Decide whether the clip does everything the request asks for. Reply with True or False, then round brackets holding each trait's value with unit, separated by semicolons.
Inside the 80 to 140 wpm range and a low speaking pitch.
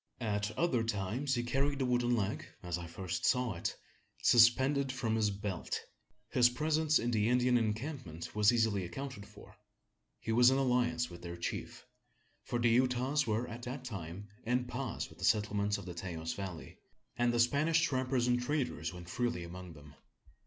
False (175 wpm; 120 Hz)